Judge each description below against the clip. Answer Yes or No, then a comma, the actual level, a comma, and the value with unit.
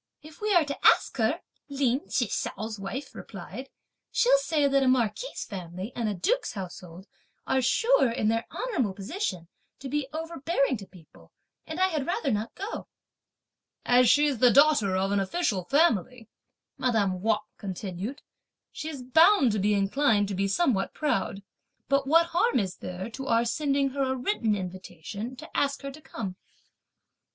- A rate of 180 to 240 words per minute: No, average, 165 wpm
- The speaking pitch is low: No, very high, 250 Hz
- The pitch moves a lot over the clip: Yes, wide, 6.6 semitones